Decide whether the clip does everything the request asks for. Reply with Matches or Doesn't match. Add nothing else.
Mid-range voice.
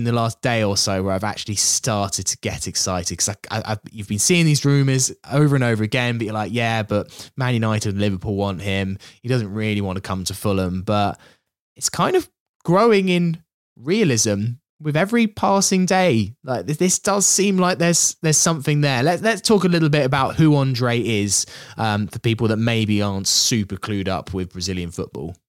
Doesn't match